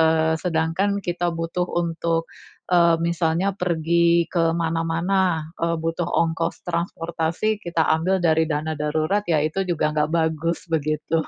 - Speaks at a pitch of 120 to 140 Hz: No, medium, 165 Hz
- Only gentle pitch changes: Yes, narrow, 1.2 semitones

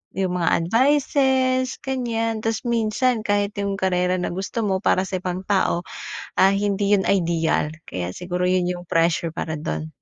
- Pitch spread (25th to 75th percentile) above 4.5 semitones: No, average, 4.1 semitones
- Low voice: No, high, 190 Hz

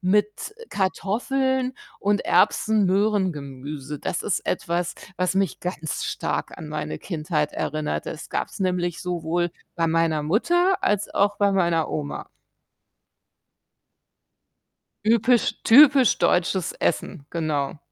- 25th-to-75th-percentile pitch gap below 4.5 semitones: No, average, 4.8 semitones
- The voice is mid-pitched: Yes, medium, 180 Hz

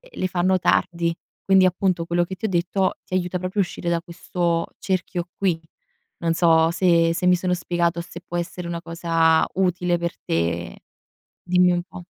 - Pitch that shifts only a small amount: Yes, narrow, 1.4 semitones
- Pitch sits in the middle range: Yes, medium, 175 Hz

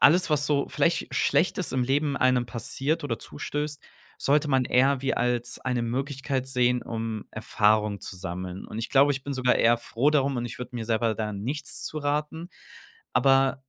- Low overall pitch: Yes, low, 130 Hz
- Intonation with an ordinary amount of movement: Yes, average, 3.4 semitones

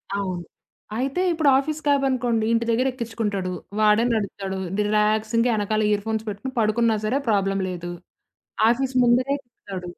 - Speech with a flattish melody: No, average, 3.5 semitones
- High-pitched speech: Yes, high, 220 Hz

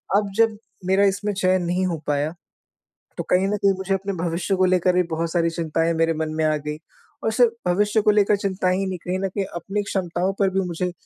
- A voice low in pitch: No, medium, 185 Hz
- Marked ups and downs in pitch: No, average, 2.8 semitones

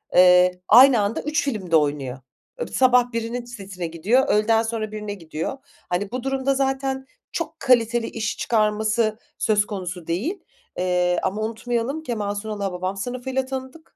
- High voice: Yes, high, 220 Hz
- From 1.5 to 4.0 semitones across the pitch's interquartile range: No, average, 5.0 semitones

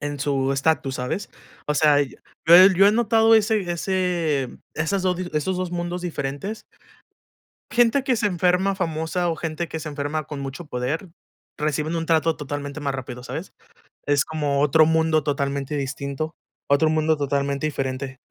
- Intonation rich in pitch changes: No, average, 3.9 semitones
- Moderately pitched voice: Yes, medium, 155 Hz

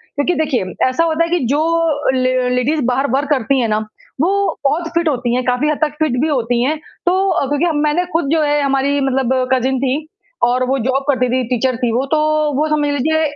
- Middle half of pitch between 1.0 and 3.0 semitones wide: No, average, 3.4 semitones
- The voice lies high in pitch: Yes, very high, 275 Hz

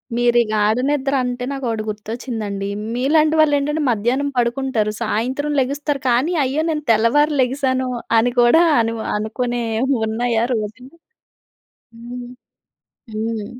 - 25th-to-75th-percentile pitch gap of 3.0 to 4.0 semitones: Yes, average, 3.6 semitones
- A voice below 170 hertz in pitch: No, high, 245 Hz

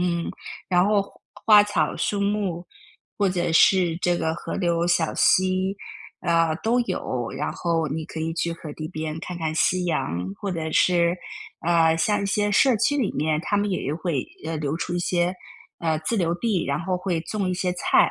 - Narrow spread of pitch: No, average, 3.0 semitones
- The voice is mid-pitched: Yes, medium, 175 Hz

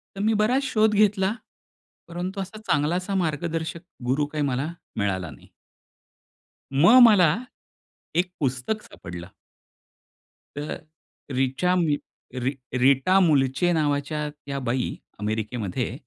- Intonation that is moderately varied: No, wide, 5.7 semitones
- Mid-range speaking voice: Yes, medium, 150 Hz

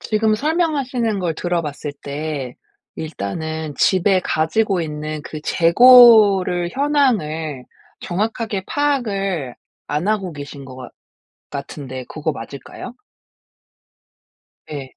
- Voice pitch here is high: No, medium, 175 Hz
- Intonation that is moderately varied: No, wide, 6.5 semitones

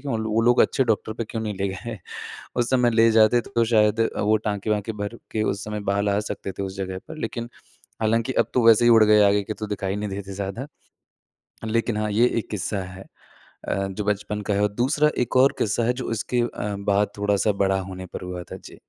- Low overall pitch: Yes, low, 105 Hz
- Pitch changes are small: Yes, narrow, 2.3 semitones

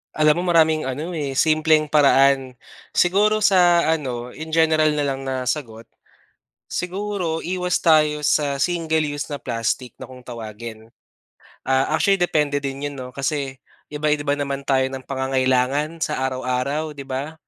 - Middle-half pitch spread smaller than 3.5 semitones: Yes, average, 3.1 semitones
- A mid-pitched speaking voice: Yes, medium, 145 Hz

